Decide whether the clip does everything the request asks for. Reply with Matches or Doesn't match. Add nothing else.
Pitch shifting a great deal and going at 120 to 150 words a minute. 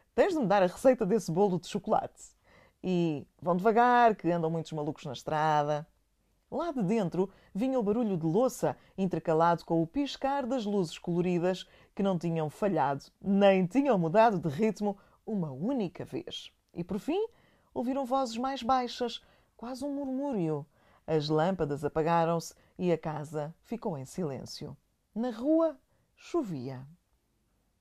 Matches